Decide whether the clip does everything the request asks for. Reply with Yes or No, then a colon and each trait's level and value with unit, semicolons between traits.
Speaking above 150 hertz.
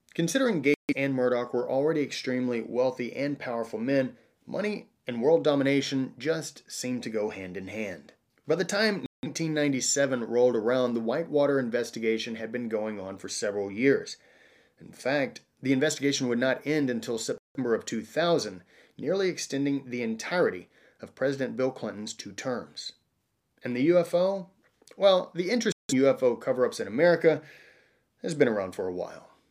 No: low, 135 Hz